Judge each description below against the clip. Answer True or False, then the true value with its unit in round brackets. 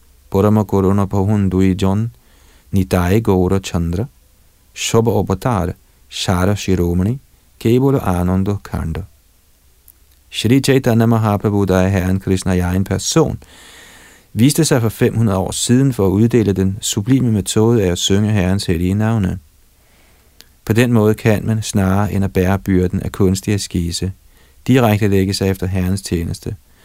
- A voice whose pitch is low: True (95 Hz)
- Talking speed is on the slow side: True (130 wpm)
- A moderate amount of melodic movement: True (3.2 semitones)